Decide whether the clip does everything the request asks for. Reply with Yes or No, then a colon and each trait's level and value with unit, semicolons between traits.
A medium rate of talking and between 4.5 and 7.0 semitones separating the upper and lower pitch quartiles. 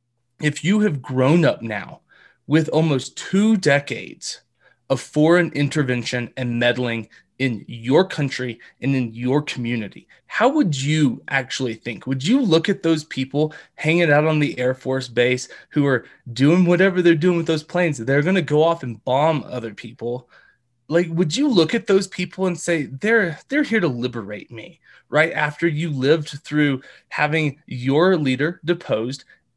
Yes: average, 165 wpm; average, 4.8 semitones